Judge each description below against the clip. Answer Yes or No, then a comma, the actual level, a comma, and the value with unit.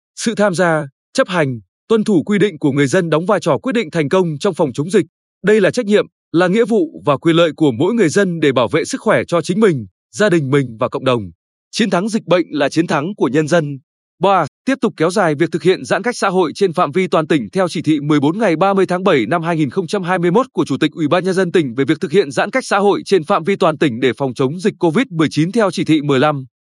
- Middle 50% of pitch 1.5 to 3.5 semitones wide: No, average, 4.9 semitones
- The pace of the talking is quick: Yes, fast, 265 wpm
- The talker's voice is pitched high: No, medium, 175 Hz